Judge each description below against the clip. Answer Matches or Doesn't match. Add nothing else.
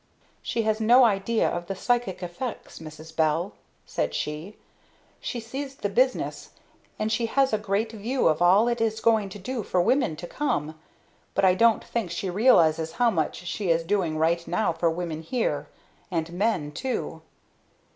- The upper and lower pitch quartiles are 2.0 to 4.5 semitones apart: Doesn't match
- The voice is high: Matches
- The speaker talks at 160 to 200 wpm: Matches